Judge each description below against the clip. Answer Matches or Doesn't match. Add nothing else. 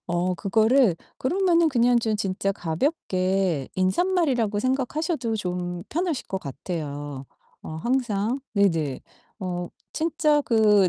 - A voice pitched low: Doesn't match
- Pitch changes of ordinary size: Doesn't match